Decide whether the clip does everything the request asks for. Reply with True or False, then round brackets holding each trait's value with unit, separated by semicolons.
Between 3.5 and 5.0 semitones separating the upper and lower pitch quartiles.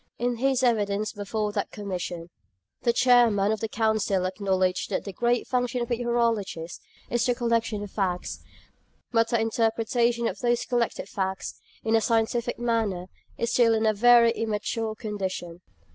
False (2.8 semitones)